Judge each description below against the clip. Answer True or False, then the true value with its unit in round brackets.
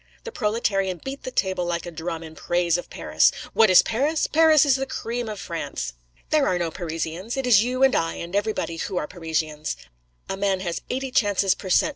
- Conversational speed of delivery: False (210 wpm)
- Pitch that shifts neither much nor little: False (6.5 semitones)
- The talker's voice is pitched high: True (195 Hz)